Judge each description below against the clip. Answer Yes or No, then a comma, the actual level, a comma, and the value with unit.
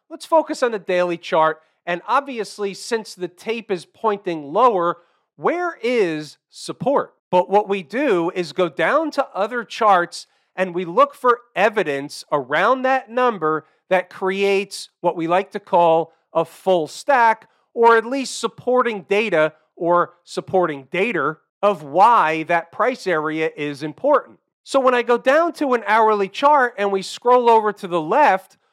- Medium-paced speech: Yes, average, 160 wpm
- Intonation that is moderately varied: No, wide, 5.8 semitones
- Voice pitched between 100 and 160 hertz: No, high, 195 Hz